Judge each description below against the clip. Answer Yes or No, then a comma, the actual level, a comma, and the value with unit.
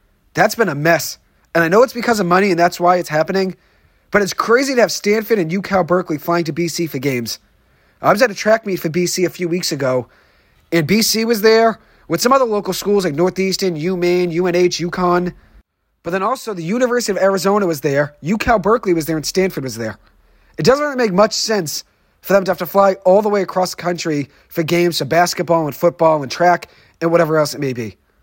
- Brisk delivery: Yes, fast, 225 wpm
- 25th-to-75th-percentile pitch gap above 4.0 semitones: No, average, 3.4 semitones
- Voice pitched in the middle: Yes, medium, 180 Hz